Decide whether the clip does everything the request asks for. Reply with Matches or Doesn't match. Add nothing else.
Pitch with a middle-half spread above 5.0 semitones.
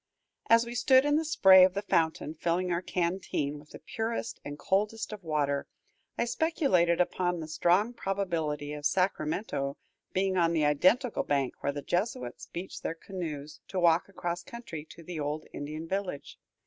Doesn't match